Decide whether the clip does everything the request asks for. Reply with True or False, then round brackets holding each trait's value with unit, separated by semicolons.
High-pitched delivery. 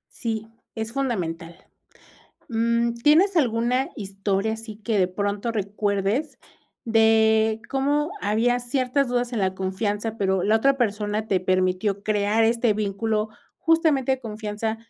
True (220 Hz)